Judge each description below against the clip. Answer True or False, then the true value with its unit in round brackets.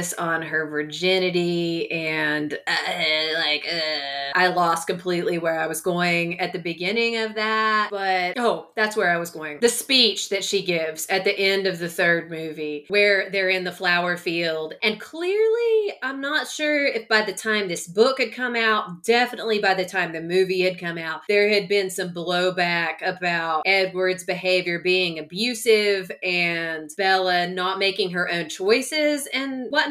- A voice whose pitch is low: False (185 Hz)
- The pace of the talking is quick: False (175 wpm)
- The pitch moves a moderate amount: True (3.9 semitones)